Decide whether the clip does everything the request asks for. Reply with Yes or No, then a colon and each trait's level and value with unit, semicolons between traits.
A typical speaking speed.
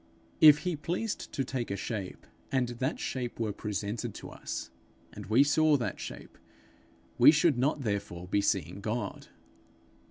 Yes: average, 155 wpm